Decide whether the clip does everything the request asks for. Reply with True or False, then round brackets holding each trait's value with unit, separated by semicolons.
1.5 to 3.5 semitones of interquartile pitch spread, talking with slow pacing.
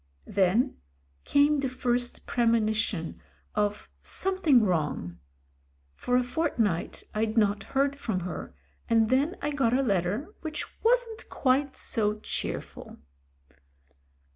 False (5.3 semitones; 115 wpm)